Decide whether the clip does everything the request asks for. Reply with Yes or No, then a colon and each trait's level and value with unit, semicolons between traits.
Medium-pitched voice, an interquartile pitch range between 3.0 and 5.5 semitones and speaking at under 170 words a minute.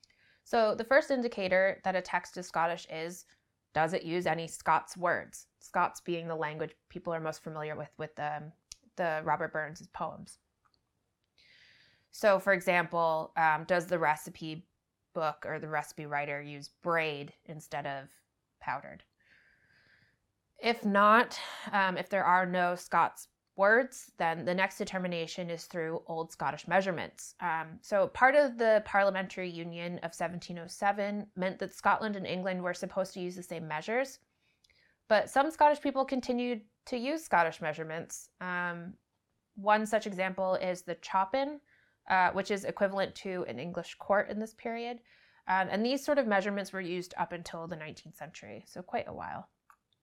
Yes: medium, 180 Hz; average, 3.8 semitones; average, 155 wpm